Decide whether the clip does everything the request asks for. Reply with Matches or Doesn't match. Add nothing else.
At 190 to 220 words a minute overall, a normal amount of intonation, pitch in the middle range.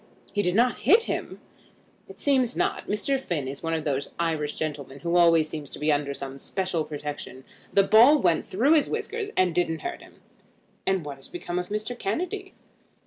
Doesn't match